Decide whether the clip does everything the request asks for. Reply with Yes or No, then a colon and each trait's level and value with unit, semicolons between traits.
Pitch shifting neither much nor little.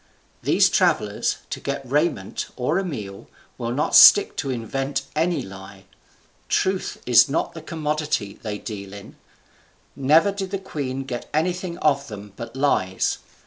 No: wide, 6.6 semitones